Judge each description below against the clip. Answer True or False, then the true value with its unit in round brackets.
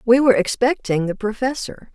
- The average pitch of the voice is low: False (230 Hz)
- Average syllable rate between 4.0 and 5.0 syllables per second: False (5.4 syllables/s)